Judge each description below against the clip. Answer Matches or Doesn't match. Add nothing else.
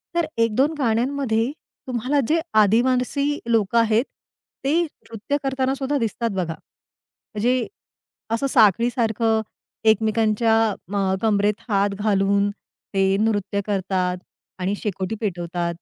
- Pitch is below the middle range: Doesn't match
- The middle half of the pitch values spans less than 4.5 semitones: Matches